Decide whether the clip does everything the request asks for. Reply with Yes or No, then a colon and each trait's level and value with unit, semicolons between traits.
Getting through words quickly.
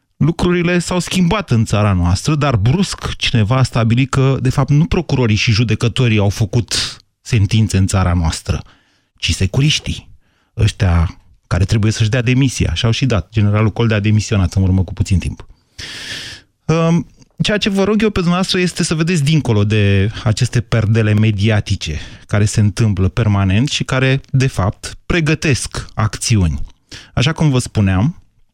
No: average, 155 wpm